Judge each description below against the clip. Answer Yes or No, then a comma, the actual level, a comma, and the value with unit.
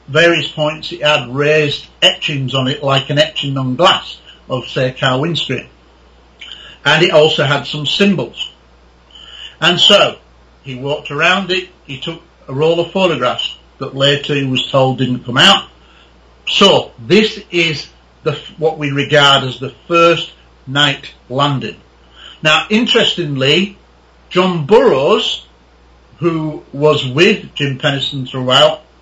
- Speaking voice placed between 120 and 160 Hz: Yes, medium, 140 Hz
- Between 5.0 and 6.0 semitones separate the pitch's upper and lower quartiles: No, average, 4.4 semitones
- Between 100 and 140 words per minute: Yes, slow, 135 wpm